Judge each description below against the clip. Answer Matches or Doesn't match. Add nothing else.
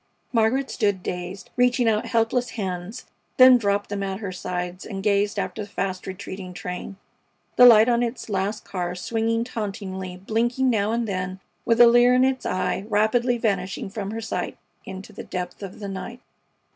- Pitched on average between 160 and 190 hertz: Doesn't match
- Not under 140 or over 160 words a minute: Doesn't match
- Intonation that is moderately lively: Matches